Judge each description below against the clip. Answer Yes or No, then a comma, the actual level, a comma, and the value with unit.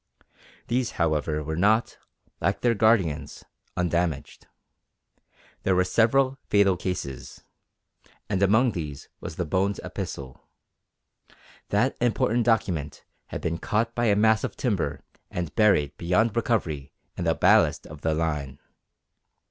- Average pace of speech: No, slow, 125 wpm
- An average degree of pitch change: No, wide, 6.1 semitones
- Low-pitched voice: Yes, very low, 95 Hz